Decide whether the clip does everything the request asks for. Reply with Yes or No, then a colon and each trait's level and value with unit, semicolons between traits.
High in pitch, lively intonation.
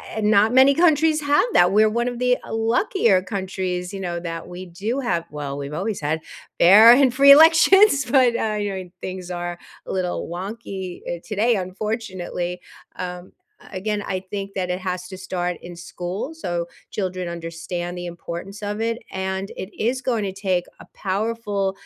No: high, 195 Hz; average, 4.3 semitones